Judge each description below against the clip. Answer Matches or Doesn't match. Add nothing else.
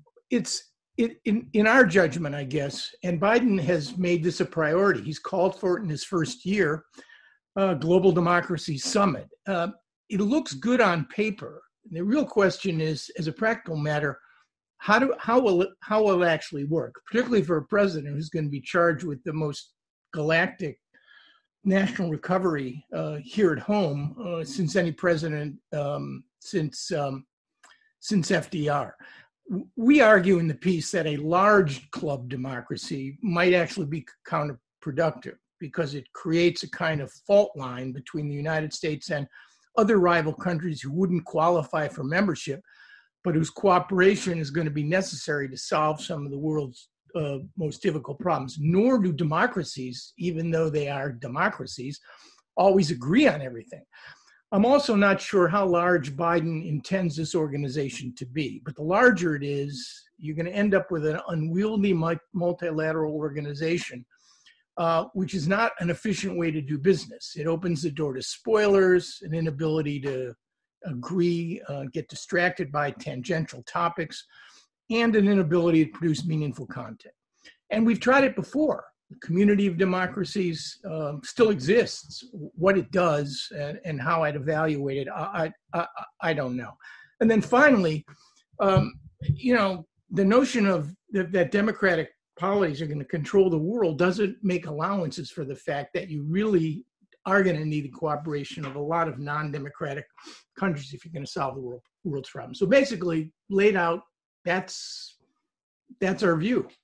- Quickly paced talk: Doesn't match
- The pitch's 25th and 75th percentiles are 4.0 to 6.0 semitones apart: Matches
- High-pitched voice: Doesn't match